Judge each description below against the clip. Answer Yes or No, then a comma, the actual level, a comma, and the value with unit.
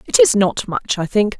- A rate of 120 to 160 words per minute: No, fast, 255 wpm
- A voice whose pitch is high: Yes, high, 215 Hz